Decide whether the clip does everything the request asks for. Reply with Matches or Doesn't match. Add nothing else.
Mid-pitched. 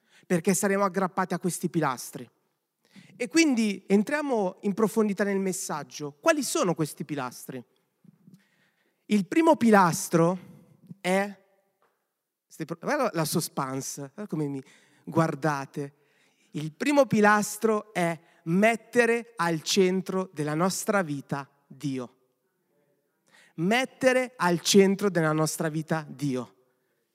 Matches